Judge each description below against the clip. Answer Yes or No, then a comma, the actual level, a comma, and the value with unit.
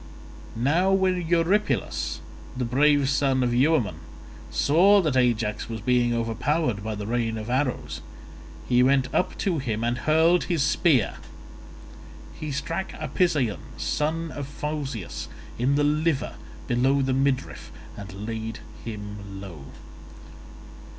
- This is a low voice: Yes, low, 130 Hz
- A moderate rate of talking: No, slow, 125 wpm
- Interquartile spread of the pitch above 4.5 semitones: Yes, average, 5.1 semitones